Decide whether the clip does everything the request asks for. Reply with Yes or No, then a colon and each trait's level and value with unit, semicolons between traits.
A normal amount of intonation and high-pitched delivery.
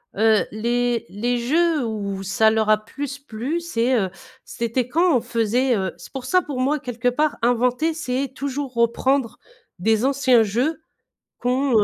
Yes: average, 3.6 semitones; high, 245 Hz